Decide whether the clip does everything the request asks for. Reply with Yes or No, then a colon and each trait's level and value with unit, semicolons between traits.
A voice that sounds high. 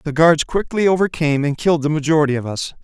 No: medium, 155 Hz